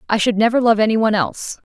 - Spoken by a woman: Yes, female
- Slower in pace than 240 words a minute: No, fast, 245 wpm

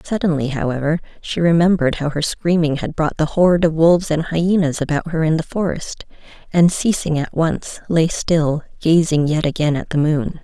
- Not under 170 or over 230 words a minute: Yes, average, 185 wpm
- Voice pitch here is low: No, medium, 160 Hz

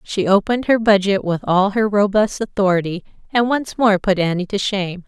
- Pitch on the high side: Yes, high, 200 Hz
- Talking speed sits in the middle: Yes, average, 190 wpm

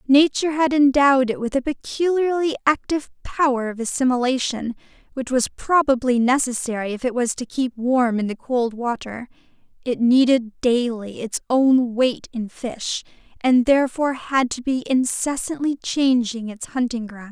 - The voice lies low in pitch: No, very high, 255 Hz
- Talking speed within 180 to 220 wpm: No, average, 150 wpm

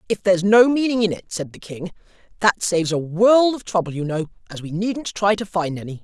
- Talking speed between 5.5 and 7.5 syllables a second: Yes, 5.6 syllables/s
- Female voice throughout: No, male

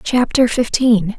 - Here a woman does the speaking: Yes, female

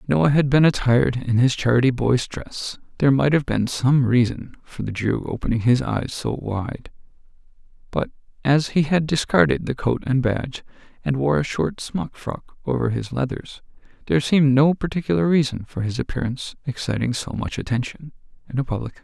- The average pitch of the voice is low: Yes, low, 130 Hz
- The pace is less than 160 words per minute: No, average, 185 wpm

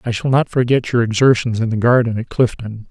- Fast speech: Yes, fast, 225 wpm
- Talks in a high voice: No, low, 120 Hz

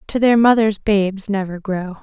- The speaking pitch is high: Yes, high, 205 Hz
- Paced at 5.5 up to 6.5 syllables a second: No, 4.8 syllables/s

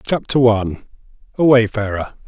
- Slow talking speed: Yes, slow, 105 wpm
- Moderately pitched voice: No, low, 115 Hz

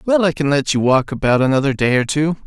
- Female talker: No, male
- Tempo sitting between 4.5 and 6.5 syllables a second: Yes, 6.2 syllables/s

